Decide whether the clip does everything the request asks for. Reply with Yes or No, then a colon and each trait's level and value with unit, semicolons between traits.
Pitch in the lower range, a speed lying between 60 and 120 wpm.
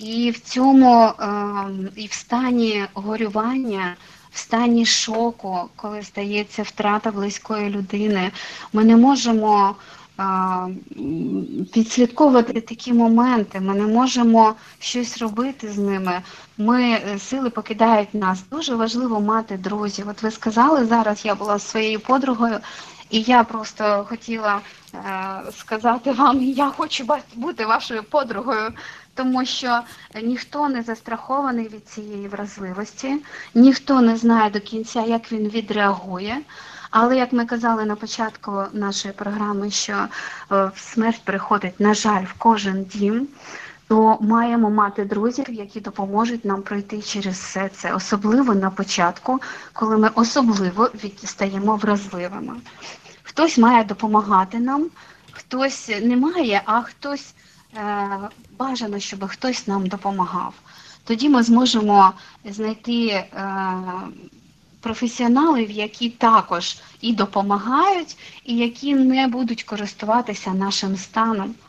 No: high, 220 Hz; average, 115 wpm